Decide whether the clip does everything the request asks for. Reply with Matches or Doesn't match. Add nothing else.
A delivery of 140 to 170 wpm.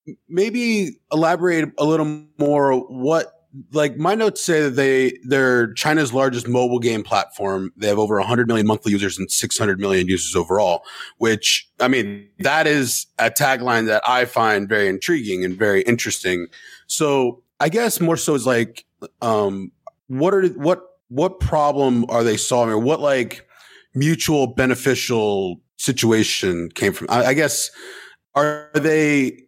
Matches